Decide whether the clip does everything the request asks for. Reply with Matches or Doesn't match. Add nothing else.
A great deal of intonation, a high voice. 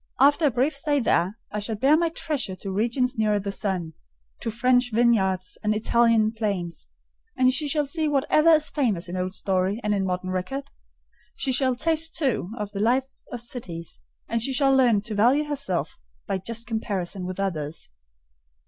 Matches